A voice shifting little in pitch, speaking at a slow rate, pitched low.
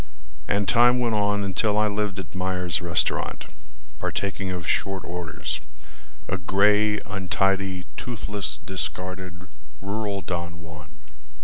Yes: narrow, 2.2 semitones; slow, 115 wpm; very low, 95 Hz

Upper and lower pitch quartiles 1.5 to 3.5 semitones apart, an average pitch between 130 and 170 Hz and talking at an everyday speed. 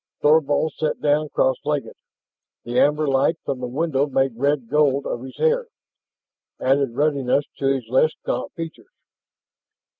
Yes: narrow, 2.4 semitones; medium, 140 Hz; average, 145 wpm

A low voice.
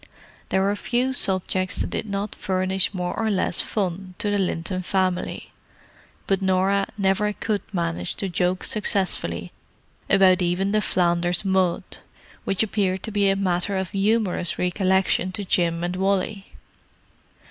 No: high, 190 Hz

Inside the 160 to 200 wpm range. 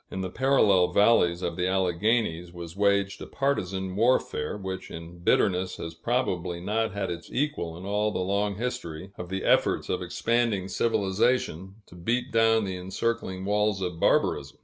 Yes: average, 165 wpm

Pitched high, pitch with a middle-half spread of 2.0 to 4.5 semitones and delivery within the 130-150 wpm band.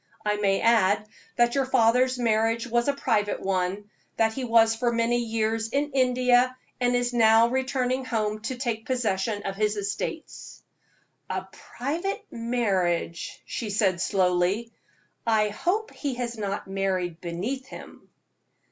Yes: high, 230 Hz; average, 3.3 semitones; average, 140 wpm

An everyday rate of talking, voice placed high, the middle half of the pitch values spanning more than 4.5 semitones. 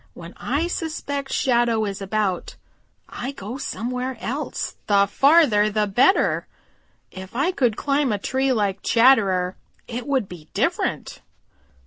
No: slow, 130 wpm; high, 235 Hz; average, 5.1 semitones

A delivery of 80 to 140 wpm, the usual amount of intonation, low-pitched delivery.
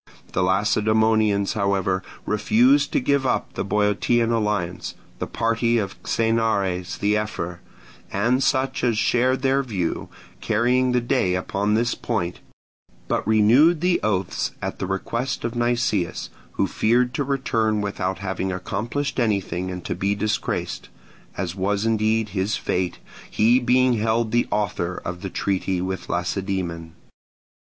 Yes: slow, 135 wpm; average, 3.8 semitones; low, 105 Hz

